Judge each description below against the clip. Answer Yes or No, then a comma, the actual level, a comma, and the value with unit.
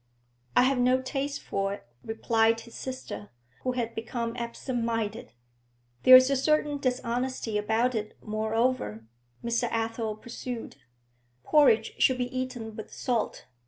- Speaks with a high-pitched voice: Yes, high, 235 Hz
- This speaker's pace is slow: Yes, slow, 130 wpm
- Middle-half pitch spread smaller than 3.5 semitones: Yes, narrow, 2.4 semitones